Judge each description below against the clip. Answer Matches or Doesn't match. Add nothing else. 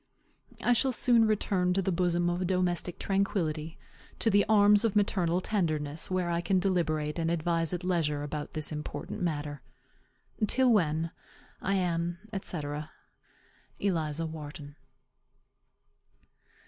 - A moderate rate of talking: Doesn't match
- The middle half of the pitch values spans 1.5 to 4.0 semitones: Matches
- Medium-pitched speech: Matches